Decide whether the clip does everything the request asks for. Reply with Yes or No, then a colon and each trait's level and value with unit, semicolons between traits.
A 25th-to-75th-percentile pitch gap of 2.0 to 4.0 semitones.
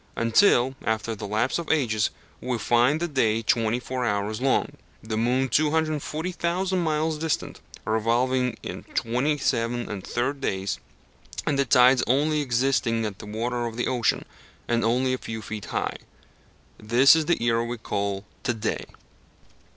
Yes: average, 3.7 semitones